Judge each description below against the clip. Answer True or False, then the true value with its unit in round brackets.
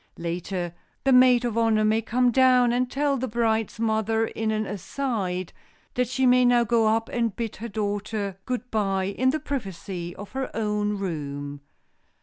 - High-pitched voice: True (220 Hz)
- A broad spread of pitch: False (3.7 semitones)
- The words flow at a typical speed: True (170 wpm)